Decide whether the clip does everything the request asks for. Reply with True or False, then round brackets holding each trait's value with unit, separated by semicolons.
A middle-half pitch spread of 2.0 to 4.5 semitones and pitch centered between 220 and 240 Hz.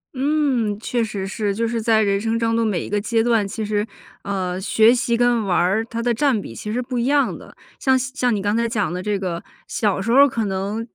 True (2.9 semitones; 225 Hz)